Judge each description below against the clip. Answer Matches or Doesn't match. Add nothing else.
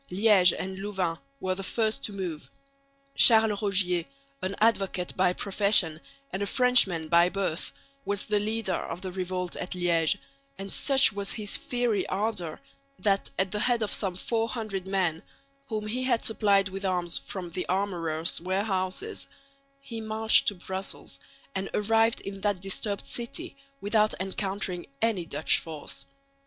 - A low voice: Doesn't match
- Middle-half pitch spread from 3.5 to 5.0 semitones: Doesn't match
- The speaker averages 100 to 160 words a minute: Matches